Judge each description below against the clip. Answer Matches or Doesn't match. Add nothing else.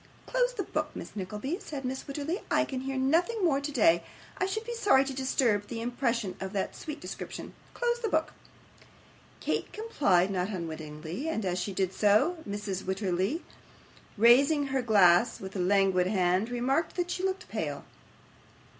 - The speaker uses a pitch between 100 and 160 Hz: Doesn't match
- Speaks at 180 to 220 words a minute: Doesn't match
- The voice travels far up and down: Matches